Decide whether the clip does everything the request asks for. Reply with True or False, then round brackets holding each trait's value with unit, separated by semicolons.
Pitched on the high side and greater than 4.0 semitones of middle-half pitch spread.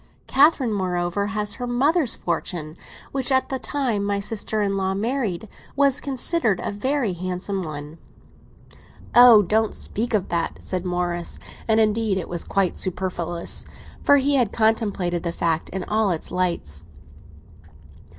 True (205 Hz; 5.3 semitones)